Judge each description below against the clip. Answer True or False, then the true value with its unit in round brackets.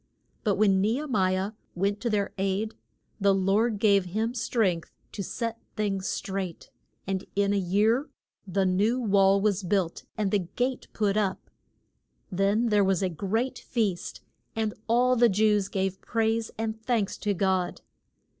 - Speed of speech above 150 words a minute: True (160 wpm)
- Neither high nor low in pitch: False (205 Hz)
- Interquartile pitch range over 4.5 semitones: False (2.6 semitones)